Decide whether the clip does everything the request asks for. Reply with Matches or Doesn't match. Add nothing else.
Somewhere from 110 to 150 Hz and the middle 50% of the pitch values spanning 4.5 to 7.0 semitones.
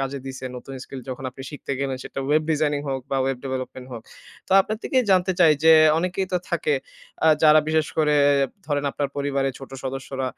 Doesn't match